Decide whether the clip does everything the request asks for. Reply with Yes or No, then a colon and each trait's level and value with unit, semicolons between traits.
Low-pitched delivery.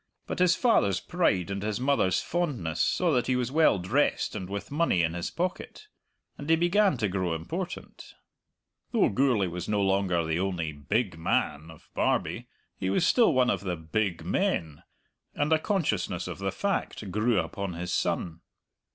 Yes: low, 100 Hz